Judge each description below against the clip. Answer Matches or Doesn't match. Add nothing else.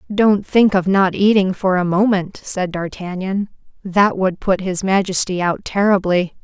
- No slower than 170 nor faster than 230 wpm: Doesn't match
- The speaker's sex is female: Matches